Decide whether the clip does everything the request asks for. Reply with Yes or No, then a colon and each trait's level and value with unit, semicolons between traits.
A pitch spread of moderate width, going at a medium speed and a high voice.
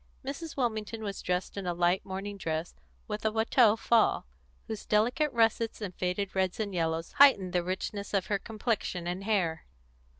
Yes: average, 3.6 semitones; average, 170 wpm; high, 200 Hz